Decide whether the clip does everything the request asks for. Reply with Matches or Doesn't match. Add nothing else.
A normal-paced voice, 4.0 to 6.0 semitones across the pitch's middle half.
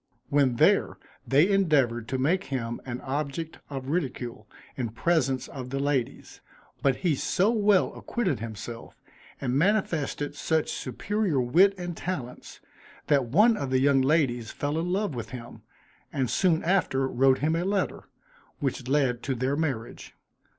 Matches